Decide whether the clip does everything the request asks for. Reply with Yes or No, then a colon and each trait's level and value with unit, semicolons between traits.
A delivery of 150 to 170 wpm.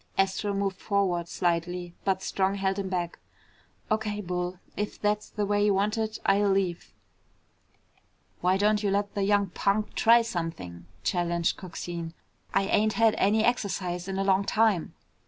Yes: average, 155 wpm